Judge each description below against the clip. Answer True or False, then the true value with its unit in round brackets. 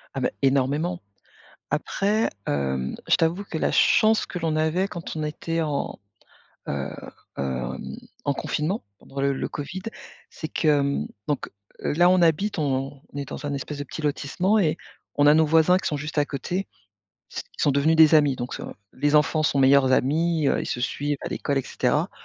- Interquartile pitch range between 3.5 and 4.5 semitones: False (2.9 semitones)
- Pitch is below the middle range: False (150 Hz)